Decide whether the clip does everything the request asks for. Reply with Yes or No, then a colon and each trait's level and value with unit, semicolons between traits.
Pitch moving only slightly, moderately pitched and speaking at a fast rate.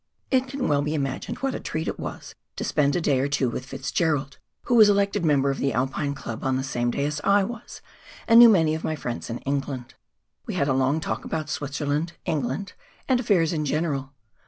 No: average, 4.4 semitones; medium, 145 Hz; fast, 220 wpm